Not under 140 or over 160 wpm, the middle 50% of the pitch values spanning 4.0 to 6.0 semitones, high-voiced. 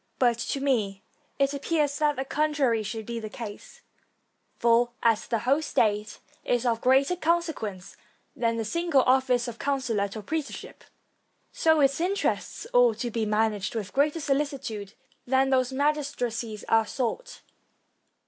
Yes: average, 150 wpm; average, 4.3 semitones; very high, 255 Hz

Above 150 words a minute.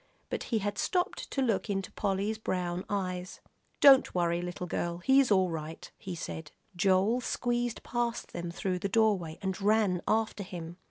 Yes: average, 165 wpm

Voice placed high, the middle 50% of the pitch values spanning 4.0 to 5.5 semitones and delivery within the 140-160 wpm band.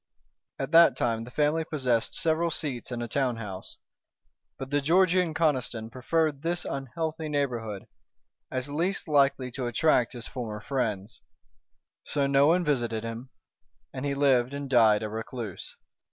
No: low, 135 Hz; average, 4.5 semitones; average, 150 wpm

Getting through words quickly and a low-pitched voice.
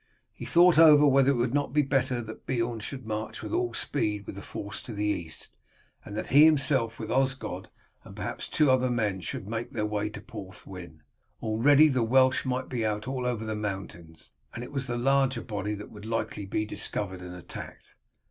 Yes: fast, 210 wpm; low, 115 Hz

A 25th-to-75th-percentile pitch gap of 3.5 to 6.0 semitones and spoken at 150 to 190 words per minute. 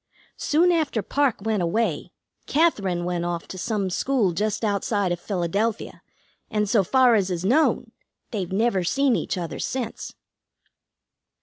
No: average, 4.9 semitones; average, 140 wpm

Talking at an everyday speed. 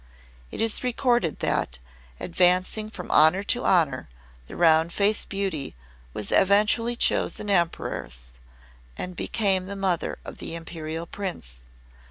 No: slow, 125 wpm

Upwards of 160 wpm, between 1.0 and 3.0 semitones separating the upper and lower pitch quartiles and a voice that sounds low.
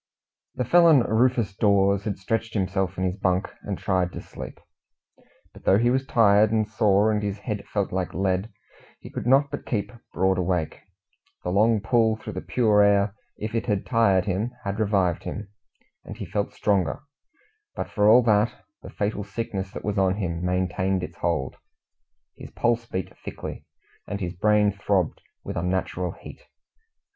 Yes: average, 170 wpm; average, 2.7 semitones; low, 100 Hz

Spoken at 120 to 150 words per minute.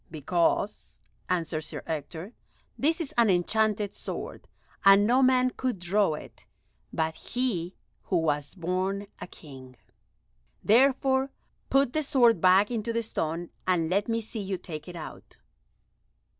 Yes: average, 140 wpm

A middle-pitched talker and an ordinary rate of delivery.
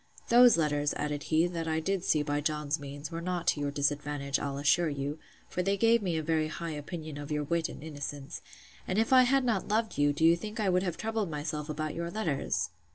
No: medium, 160 Hz; fast, 230 wpm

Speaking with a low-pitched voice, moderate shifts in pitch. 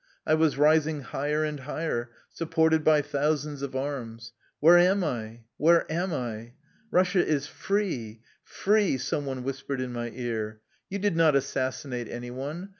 No: medium, 145 Hz; average, 4.5 semitones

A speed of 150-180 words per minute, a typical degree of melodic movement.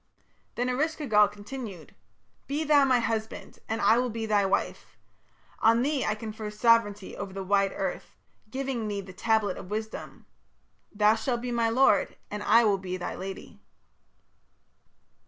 Yes: average, 160 wpm; average, 3.0 semitones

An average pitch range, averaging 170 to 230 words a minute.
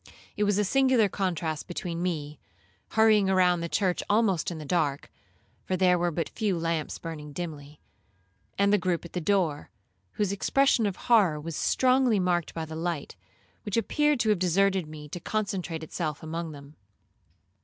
Yes: average, 4.1 semitones; average, 175 wpm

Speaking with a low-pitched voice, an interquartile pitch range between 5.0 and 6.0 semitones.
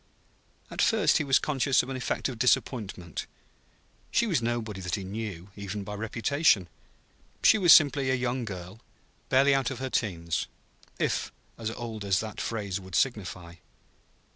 Yes: low, 115 Hz; average, 5.3 semitones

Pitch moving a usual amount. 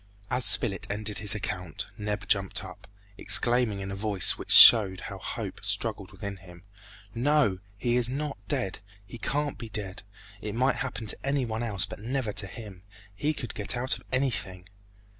Yes: average, 4.0 semitones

